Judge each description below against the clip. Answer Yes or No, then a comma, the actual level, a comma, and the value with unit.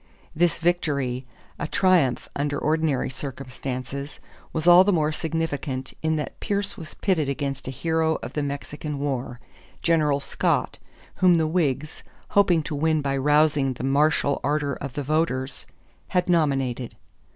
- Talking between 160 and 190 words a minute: No, average, 145 wpm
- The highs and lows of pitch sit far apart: No, average, 2.9 semitones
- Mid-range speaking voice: Yes, medium, 150 Hz